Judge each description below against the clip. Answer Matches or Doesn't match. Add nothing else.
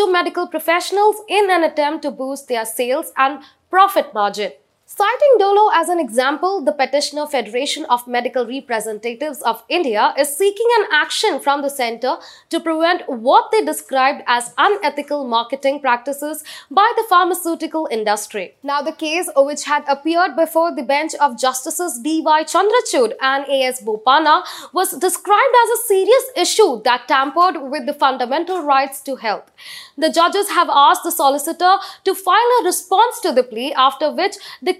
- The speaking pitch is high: Matches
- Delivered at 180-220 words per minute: Doesn't match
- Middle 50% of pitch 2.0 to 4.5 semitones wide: Doesn't match